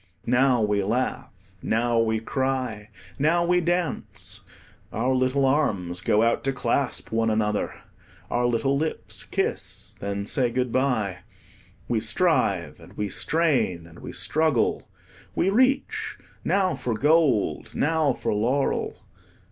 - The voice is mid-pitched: No, low, 125 Hz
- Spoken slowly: Yes, slow, 130 wpm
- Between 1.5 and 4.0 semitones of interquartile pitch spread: No, average, 5.0 semitones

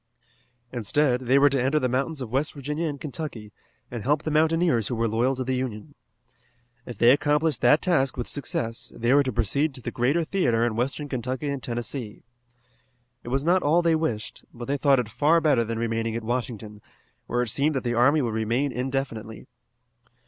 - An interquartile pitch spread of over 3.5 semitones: Yes, average, 3.9 semitones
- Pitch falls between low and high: No, low, 130 Hz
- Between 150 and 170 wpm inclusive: No, average, 200 wpm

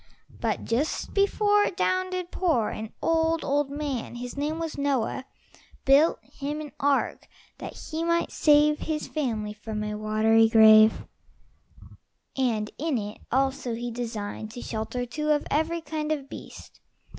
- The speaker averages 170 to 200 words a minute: No, average, 150 wpm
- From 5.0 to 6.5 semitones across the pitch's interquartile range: Yes, wide, 5.6 semitones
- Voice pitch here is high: Yes, very high, 280 Hz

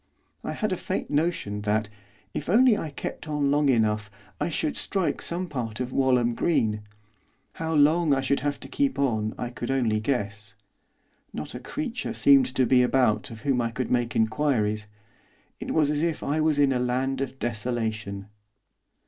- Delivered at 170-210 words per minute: Yes, average, 180 wpm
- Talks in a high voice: No, low, 130 Hz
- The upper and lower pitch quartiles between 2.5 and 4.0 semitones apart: No, average, 5.1 semitones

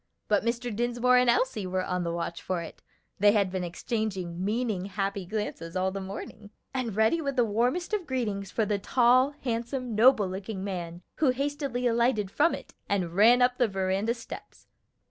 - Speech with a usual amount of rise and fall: Yes, average, 4.5 semitones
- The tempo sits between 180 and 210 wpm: Yes, average, 185 wpm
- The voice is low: No, high, 215 Hz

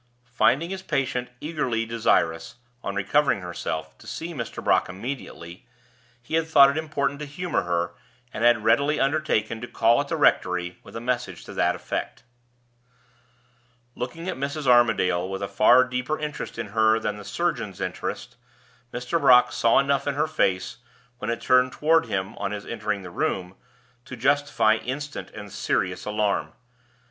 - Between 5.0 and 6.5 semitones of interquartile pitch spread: Yes, wide, 5.6 semitones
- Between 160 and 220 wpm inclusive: Yes, average, 165 wpm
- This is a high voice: No, low, 120 Hz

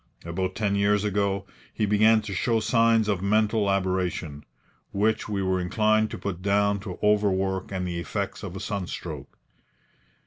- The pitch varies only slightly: Yes, narrow, 2.2 semitones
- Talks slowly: No, average, 160 wpm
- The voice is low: Yes, low, 100 Hz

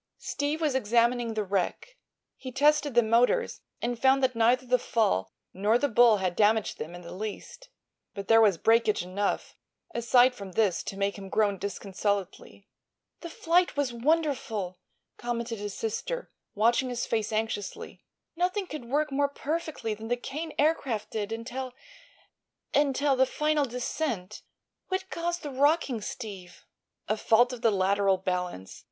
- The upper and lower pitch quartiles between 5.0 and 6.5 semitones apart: Yes, wide, 5.4 semitones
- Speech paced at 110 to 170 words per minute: Yes, average, 150 wpm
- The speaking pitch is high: Yes, high, 235 Hz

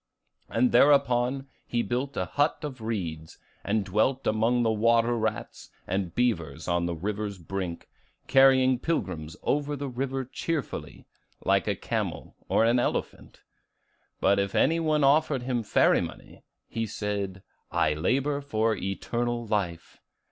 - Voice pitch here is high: No, low, 115 Hz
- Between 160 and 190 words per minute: No, average, 140 wpm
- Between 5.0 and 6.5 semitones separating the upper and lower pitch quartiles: Yes, average, 5.3 semitones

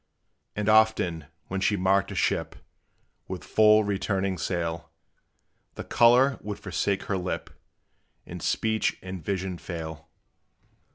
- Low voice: Yes, very low, 95 Hz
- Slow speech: Yes, slow, 120 wpm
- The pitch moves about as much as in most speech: Yes, average, 3.3 semitones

